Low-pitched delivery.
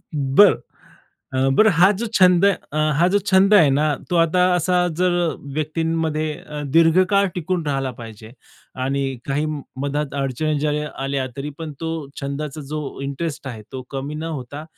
No: medium, 155 Hz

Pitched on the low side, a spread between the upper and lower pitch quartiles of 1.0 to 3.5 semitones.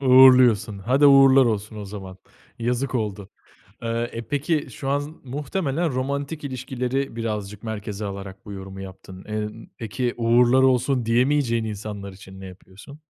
No: low, 115 Hz; average, 4.5 semitones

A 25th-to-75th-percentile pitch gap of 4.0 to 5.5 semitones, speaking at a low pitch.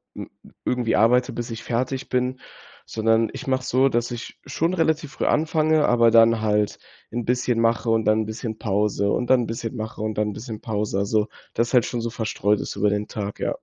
No: narrow, 2.6 semitones; low, 115 Hz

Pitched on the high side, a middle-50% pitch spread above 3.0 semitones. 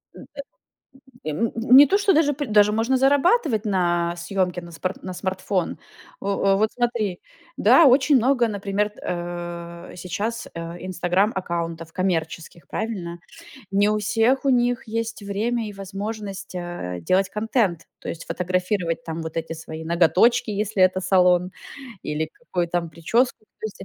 Yes: high, 195 Hz; average, 4.7 semitones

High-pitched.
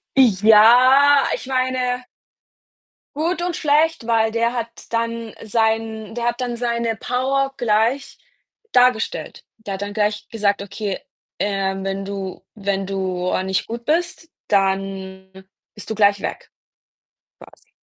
Yes: high, 225 Hz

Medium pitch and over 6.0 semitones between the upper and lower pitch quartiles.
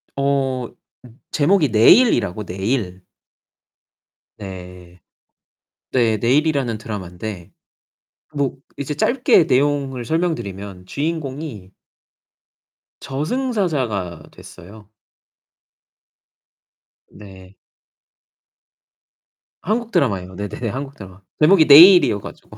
No: low, 125 Hz; wide, 7.2 semitones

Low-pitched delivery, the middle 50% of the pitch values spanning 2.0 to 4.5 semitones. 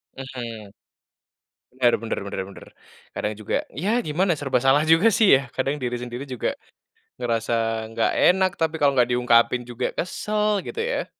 No: low, 130 Hz; wide, 5.5 semitones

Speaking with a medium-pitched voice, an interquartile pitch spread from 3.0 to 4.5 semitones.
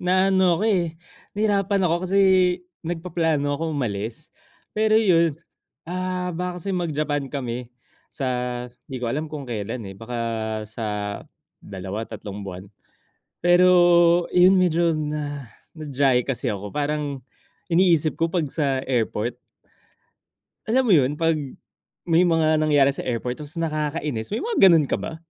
No: medium, 155 Hz; wide, 5.6 semitones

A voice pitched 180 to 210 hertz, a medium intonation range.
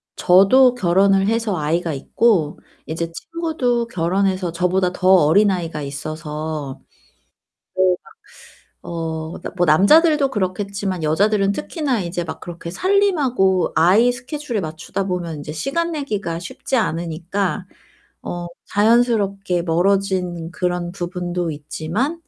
Yes: medium, 185 Hz; average, 4.8 semitones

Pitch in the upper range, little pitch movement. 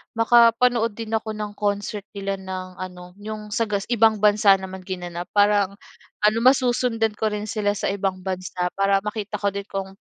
Yes: high, 205 Hz; narrow, 2.3 semitones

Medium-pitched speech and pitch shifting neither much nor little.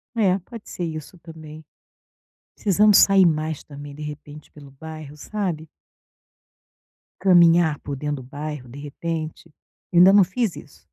Yes: medium, 155 Hz; average, 3.5 semitones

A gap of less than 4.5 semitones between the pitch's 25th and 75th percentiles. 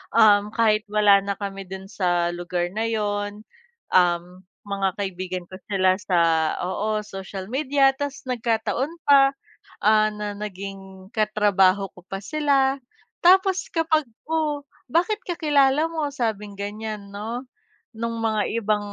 No: wide, 5.5 semitones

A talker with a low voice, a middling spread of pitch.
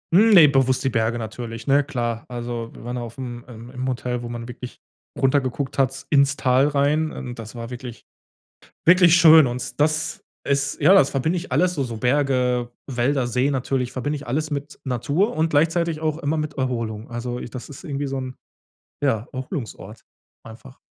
Yes: low, 130 Hz; average, 3.4 semitones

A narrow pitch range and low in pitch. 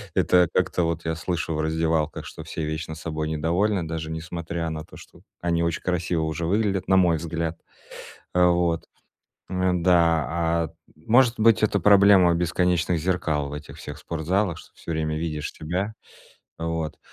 Yes: narrow, 2.1 semitones; very low, 85 Hz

